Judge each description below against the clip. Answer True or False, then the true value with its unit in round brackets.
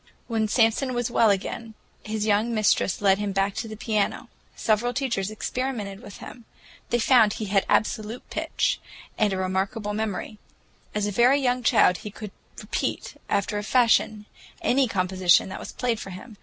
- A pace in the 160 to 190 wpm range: True (170 wpm)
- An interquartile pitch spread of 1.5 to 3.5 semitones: True (2.9 semitones)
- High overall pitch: True (215 Hz)